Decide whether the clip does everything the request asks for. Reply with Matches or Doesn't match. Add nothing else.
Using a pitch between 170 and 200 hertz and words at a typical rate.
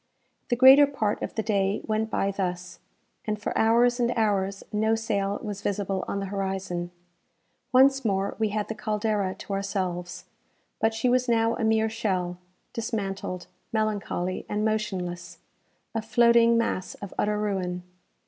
Doesn't match